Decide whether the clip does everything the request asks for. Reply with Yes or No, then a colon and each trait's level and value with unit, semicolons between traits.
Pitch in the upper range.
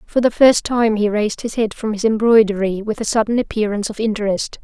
Yes: high, 215 Hz